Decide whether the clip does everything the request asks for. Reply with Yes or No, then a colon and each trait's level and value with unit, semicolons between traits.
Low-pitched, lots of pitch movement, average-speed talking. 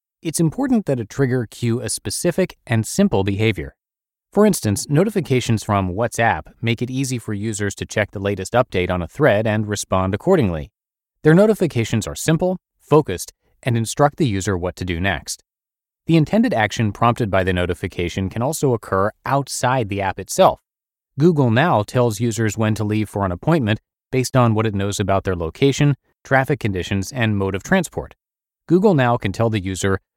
Yes: low, 115 Hz; wide, 5.8 semitones; average, 175 wpm